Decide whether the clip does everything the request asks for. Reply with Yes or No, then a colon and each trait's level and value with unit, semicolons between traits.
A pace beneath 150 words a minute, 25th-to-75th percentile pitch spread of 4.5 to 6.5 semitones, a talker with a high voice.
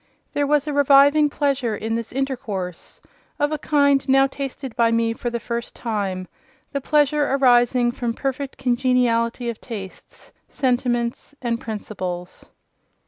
No: slow, 135 wpm; average, 3.1 semitones; very high, 250 Hz